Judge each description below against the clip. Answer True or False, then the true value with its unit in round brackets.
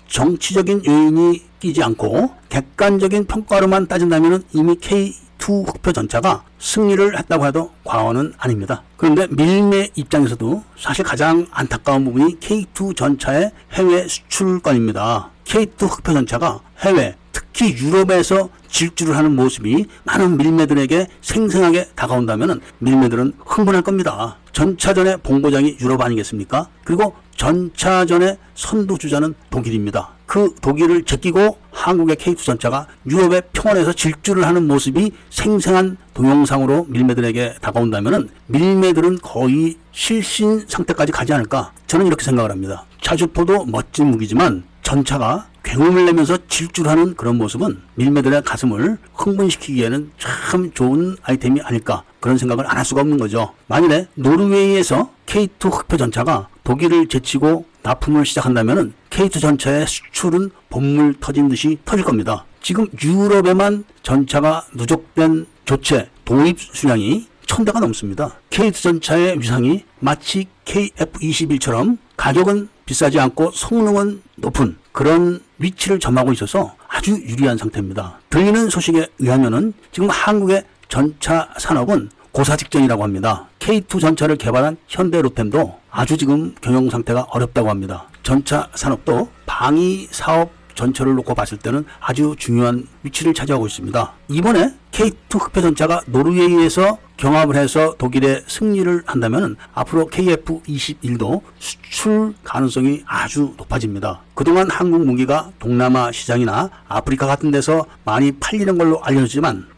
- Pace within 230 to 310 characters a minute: False (325 characters per minute)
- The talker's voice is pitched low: False (155 Hz)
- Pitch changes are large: True (5.9 semitones)